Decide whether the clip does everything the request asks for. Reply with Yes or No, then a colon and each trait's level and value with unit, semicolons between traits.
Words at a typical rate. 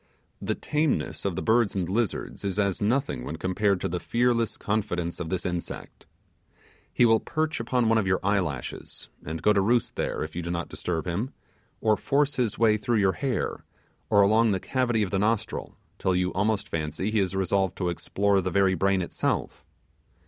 Yes: average, 195 wpm